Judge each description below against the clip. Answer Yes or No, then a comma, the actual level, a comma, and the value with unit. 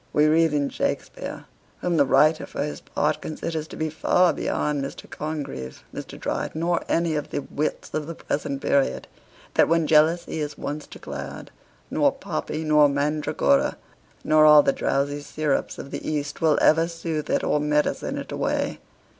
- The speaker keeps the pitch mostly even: Yes, narrow, 1.6 semitones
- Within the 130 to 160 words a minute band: No, average, 170 wpm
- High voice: No, medium, 150 Hz